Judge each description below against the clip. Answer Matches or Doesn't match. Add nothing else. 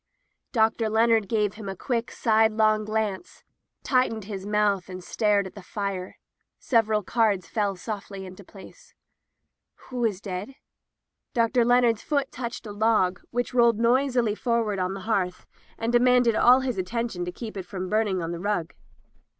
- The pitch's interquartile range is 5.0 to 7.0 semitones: Doesn't match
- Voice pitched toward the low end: Doesn't match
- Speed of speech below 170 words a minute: Matches